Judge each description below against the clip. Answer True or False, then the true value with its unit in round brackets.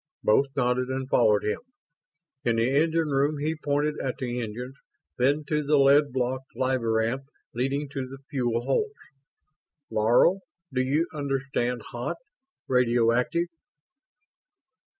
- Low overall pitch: True (130 Hz)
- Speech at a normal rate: False (125 wpm)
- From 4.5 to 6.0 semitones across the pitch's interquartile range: False (2.9 semitones)